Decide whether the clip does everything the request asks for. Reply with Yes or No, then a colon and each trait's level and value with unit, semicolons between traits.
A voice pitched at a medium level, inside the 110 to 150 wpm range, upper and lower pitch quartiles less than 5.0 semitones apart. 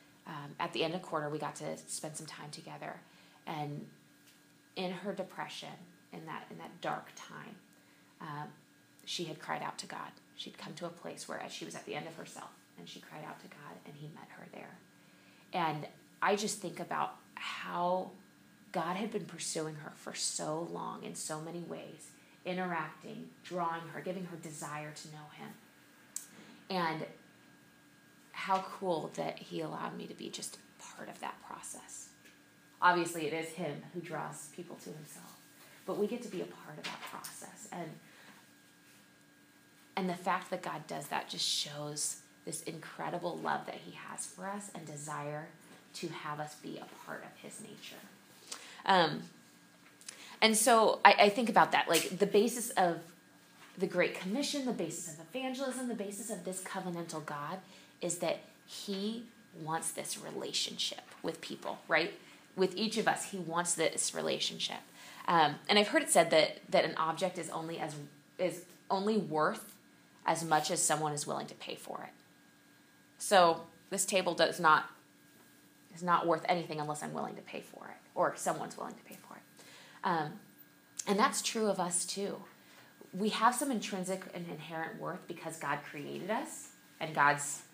No: medium, 175 Hz; average, 175 wpm; average, 3.8 semitones